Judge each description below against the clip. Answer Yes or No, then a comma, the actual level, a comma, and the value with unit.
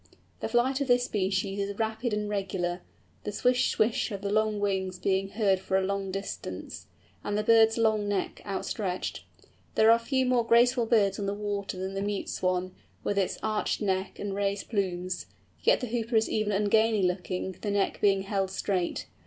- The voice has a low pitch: No, high, 205 Hz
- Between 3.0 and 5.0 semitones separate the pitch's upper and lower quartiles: No, narrow, 2.4 semitones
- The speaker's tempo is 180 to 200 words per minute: Yes, average, 185 wpm